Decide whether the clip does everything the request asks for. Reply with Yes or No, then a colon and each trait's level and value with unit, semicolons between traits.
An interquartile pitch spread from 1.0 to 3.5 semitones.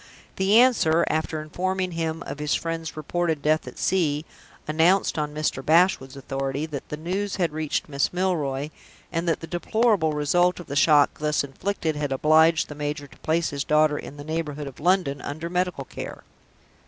Yes: average, 3.0 semitones